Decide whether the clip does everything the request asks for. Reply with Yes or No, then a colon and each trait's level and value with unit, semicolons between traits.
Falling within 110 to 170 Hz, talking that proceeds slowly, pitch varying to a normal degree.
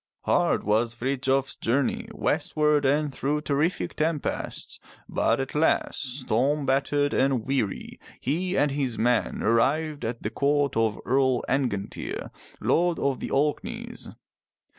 Yes: medium, 140 Hz; slow, 125 wpm; average, 3.1 semitones